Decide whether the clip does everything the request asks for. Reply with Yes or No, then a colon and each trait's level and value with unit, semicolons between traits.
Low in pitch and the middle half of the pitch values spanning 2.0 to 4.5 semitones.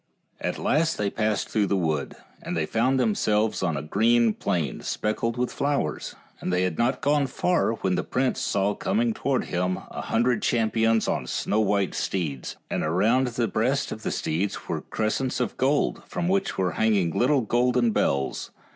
No: low, 110 Hz; average, 5.1 semitones